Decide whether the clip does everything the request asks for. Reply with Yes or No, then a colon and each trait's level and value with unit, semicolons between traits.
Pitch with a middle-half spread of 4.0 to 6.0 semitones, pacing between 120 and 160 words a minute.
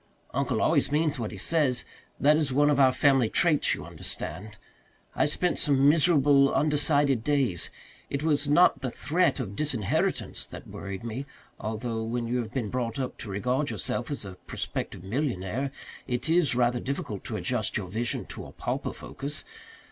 No: average, 4.5 semitones; average, 170 wpm